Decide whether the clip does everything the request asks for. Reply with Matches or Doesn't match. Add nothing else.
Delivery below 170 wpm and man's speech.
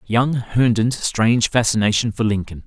Matches